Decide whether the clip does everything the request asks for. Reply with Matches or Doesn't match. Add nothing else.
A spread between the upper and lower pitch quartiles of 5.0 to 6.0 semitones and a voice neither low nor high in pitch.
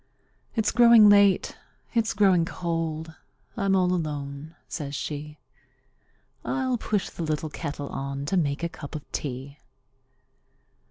Matches